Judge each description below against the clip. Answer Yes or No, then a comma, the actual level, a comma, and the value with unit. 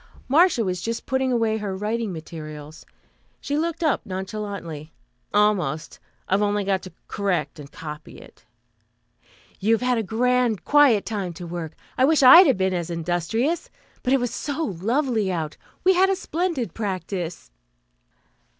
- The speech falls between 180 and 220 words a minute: No, average, 150 wpm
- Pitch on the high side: Yes, high, 210 Hz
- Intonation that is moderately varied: No, wide, 6.5 semitones